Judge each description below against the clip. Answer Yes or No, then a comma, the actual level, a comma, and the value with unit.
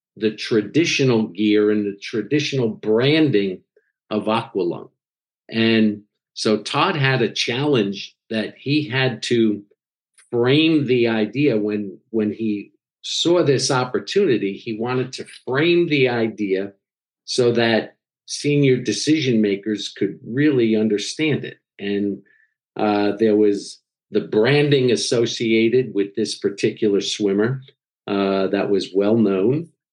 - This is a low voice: Yes, low, 115 Hz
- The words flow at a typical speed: No, slow, 120 wpm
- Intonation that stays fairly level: No, average, 4.2 semitones